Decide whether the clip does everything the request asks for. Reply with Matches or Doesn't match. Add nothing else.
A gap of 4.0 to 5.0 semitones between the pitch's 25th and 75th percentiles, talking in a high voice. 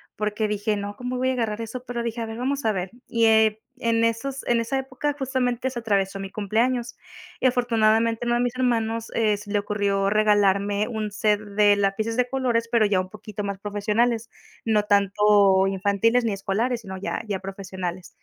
Doesn't match